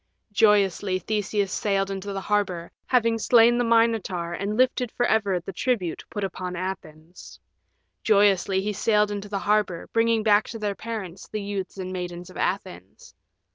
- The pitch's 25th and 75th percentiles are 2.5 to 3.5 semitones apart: Yes, average, 2.8 semitones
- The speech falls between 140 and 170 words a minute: Yes, average, 160 wpm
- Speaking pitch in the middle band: No, high, 200 Hz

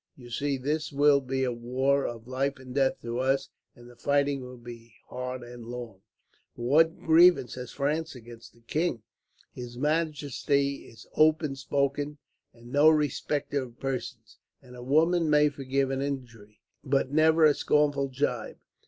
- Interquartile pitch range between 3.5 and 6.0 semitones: No, average, 3.0 semitones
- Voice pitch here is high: No, low, 135 Hz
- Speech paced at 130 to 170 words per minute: Yes, average, 160 wpm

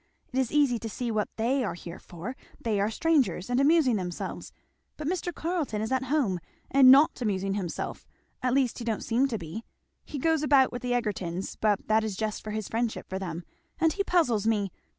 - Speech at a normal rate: No, fast, 210 wpm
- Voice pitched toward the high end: Yes, high, 230 Hz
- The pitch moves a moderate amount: Yes, average, 4.9 semitones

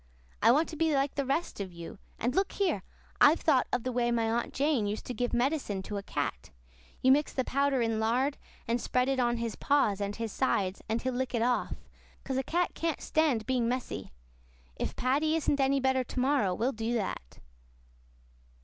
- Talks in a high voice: Yes, very high, 250 Hz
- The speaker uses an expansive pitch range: No, average, 3.5 semitones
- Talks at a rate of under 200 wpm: No, fast, 205 wpm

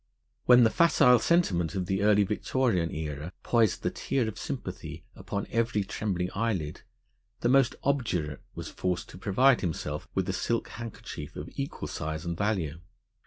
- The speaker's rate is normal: Yes, average, 160 wpm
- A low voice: Yes, low, 100 Hz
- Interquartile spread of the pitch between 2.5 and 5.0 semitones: No, wide, 5.6 semitones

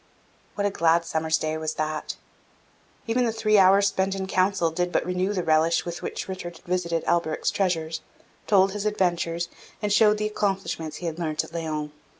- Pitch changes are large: No, average, 3.3 semitones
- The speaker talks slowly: No, average, 180 wpm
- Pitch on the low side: No, medium, 175 Hz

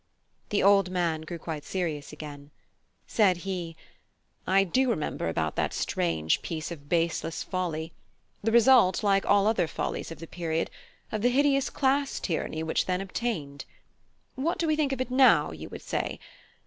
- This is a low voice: No, medium, 185 Hz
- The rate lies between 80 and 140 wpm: No, average, 165 wpm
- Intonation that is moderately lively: No, wide, 6.6 semitones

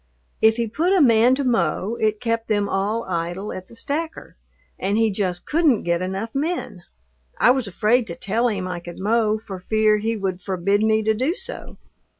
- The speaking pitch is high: Yes, high, 215 Hz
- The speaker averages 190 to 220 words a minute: Yes, average, 195 wpm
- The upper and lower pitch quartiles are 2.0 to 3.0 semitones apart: No, average, 3.4 semitones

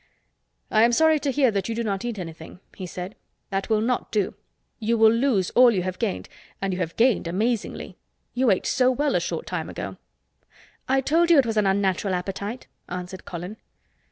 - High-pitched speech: Yes, high, 215 Hz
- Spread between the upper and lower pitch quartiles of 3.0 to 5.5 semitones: Yes, average, 4.7 semitones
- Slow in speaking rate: No, average, 195 wpm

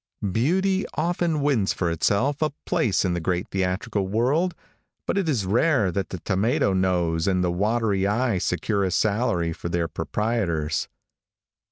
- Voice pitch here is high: No, low, 100 Hz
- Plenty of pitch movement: Yes, wide, 5.9 semitones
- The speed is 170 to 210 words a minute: No, average, 155 wpm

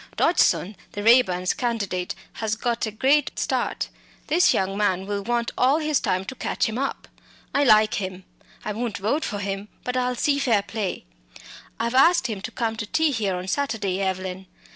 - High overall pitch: Yes, high, 220 Hz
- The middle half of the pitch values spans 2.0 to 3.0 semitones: No, average, 4.5 semitones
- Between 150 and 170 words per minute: No, average, 185 wpm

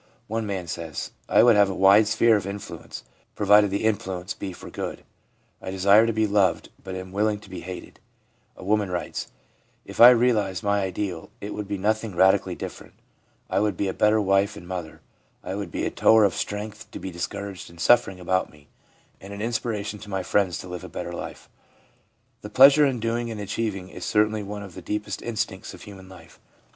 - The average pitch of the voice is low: Yes, low, 100 Hz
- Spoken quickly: Yes, fast, 210 wpm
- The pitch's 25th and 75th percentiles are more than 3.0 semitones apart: No, narrow, 2.4 semitones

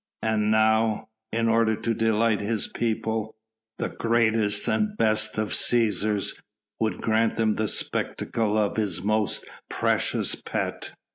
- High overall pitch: No, low, 110 Hz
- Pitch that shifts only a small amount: Yes, narrow, 1.1 semitones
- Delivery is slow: Yes, slow, 130 wpm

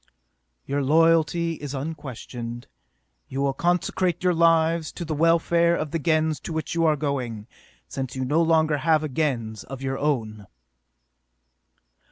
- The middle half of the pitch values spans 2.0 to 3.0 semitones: No, average, 3.7 semitones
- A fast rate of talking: No, average, 150 wpm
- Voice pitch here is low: No, medium, 155 Hz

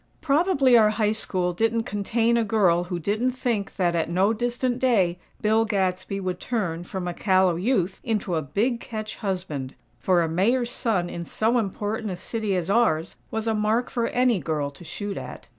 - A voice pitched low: No, high, 205 Hz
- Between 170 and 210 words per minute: Yes, average, 190 wpm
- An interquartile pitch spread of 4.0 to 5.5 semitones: Yes, average, 4.4 semitones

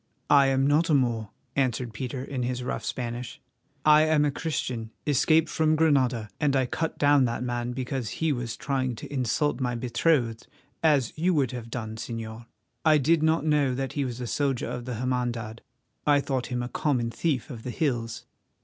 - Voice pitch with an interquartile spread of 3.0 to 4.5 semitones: Yes, average, 3.4 semitones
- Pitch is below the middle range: Yes, low, 130 Hz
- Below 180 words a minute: No, average, 190 wpm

